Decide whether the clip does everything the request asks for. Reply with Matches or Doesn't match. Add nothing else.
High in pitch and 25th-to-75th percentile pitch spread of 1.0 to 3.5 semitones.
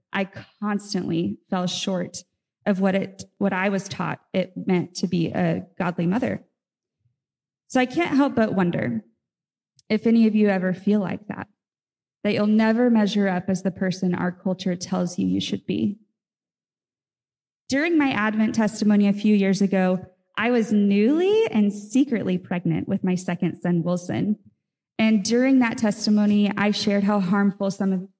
Matches